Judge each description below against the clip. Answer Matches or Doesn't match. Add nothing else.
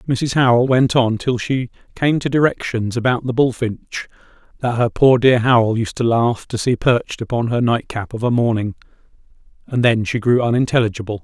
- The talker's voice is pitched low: Matches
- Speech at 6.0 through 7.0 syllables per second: Doesn't match